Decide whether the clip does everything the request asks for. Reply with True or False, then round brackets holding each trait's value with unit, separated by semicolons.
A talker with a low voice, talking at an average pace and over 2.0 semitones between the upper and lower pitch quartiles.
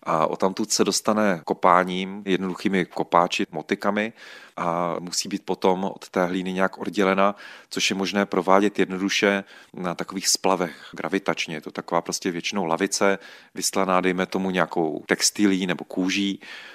False (95 Hz; 145 wpm; 1.4 semitones)